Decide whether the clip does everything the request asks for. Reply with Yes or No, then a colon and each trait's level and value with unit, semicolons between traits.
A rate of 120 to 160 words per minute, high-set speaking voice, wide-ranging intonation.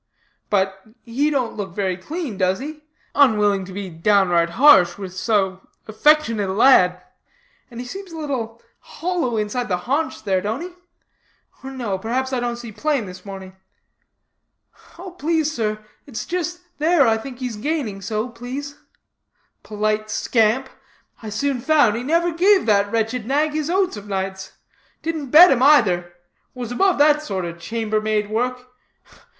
Yes: average, 155 wpm; high, 230 Hz; wide, 6.3 semitones